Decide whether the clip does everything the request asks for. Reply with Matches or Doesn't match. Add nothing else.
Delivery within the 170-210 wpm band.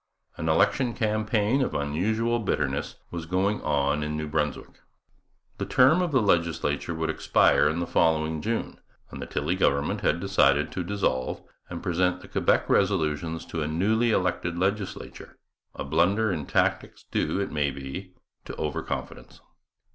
Doesn't match